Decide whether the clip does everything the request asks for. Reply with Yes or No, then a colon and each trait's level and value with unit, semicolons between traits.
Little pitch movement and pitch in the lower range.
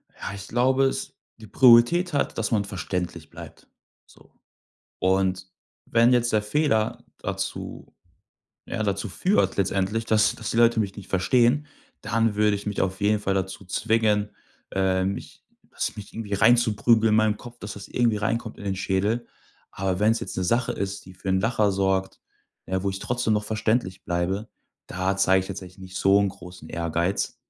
No: average, 3.1 semitones; low, 105 Hz